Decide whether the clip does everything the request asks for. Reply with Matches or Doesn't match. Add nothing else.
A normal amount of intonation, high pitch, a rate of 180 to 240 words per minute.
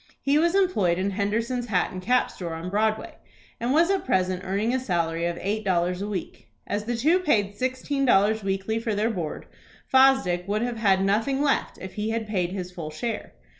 Matches